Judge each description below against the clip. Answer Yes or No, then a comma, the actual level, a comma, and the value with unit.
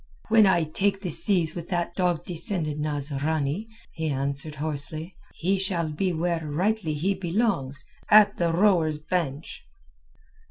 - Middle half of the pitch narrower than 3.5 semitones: No, average, 3.9 semitones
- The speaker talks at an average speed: No, slow, 130 wpm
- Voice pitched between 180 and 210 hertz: No, medium, 165 Hz